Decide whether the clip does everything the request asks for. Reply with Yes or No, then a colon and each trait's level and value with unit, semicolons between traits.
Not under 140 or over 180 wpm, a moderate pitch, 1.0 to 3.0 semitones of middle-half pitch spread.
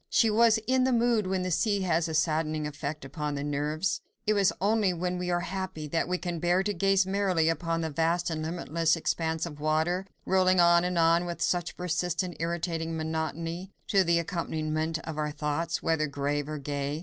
No: average, 200 wpm; medium, 170 Hz; average, 2.7 semitones